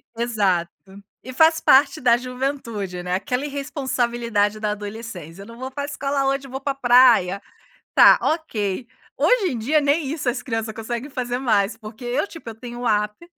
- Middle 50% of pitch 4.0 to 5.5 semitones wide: Yes, average, 4.3 semitones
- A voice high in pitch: Yes, high, 245 Hz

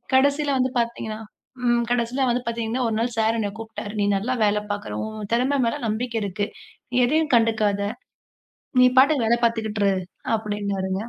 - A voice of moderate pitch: No, high, 225 Hz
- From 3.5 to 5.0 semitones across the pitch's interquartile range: No, average, 2.7 semitones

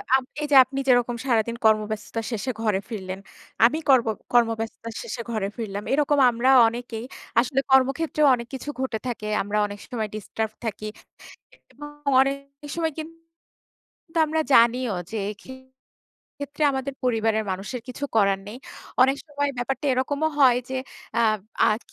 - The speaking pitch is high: Yes, high, 240 Hz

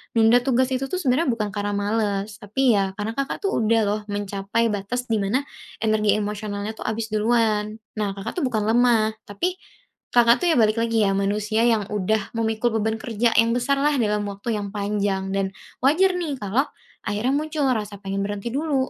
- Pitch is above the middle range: Yes, high, 220 Hz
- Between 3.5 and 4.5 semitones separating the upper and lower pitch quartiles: No, average, 2.9 semitones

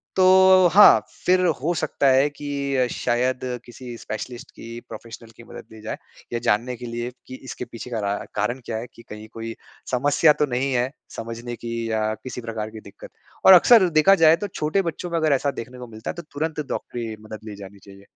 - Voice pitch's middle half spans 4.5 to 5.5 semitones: Yes, average, 4.8 semitones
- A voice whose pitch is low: Yes, low, 125 Hz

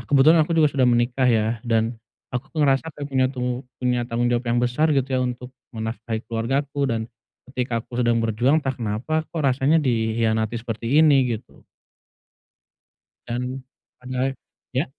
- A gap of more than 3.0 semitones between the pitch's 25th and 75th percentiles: No, narrow, 2.6 semitones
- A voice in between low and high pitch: No, low, 125 Hz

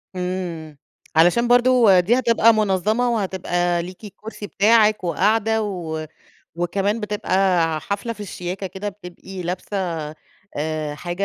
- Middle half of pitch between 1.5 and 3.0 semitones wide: No, average, 3.6 semitones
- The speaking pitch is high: Yes, high, 195 Hz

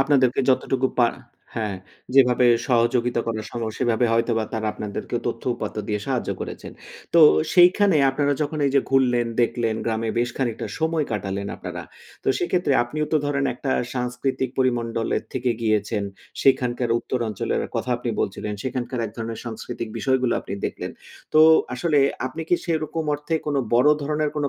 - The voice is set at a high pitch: No, low, 125 Hz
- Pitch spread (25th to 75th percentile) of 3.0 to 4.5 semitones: Yes, average, 3.6 semitones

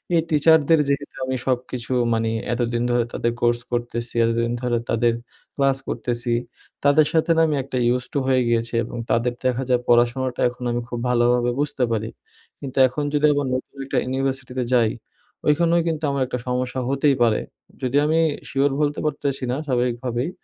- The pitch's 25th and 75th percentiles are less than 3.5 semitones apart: Yes, average, 2.7 semitones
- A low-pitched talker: Yes, low, 125 Hz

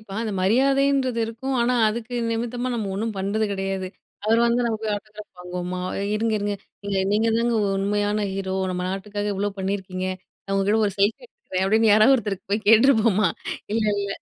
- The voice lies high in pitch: Yes, high, 210 Hz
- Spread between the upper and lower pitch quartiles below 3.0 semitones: Yes, narrow, 2.6 semitones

